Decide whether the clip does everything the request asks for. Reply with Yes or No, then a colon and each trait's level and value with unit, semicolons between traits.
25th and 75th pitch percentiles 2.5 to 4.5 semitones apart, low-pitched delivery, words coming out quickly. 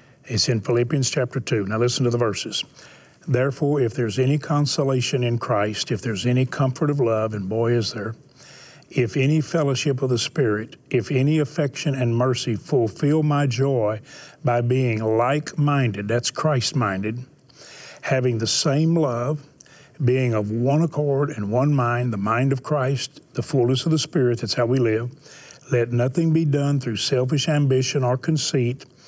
No: average, 3.2 semitones; low, 130 Hz; average, 165 wpm